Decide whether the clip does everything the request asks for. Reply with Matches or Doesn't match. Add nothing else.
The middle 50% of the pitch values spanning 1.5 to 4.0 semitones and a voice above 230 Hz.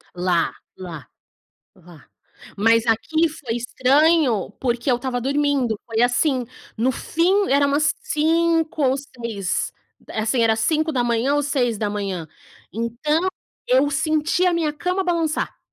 Doesn't match